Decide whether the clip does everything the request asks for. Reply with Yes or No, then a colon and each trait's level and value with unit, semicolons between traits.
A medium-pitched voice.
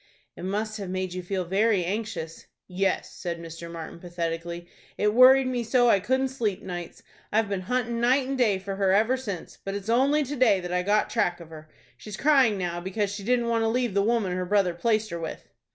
No: high, 200 Hz